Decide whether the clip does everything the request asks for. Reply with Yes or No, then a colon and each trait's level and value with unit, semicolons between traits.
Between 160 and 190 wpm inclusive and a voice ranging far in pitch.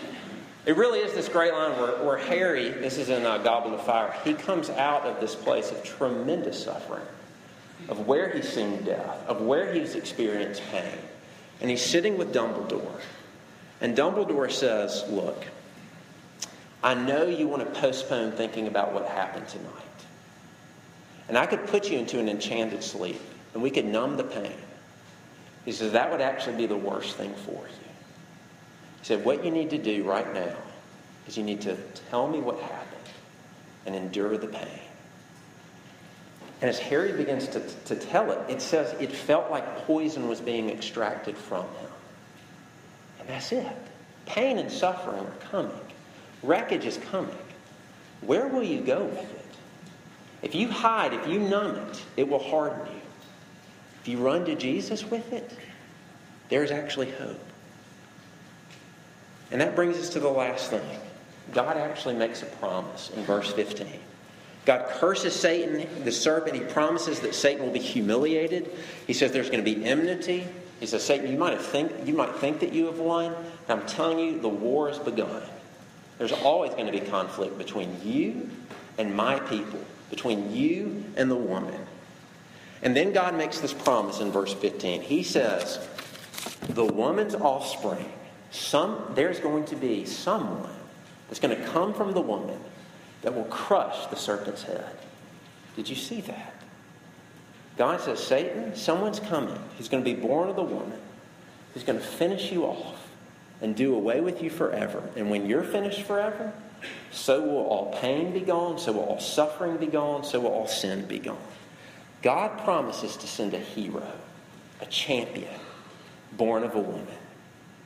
Yes: average, 165 wpm; wide, 7.5 semitones